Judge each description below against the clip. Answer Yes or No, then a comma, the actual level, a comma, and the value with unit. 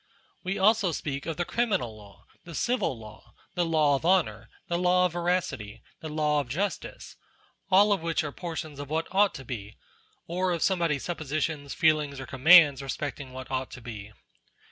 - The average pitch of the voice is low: No, medium, 155 Hz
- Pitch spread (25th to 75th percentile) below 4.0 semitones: No, average, 5.0 semitones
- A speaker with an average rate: Yes, average, 185 wpm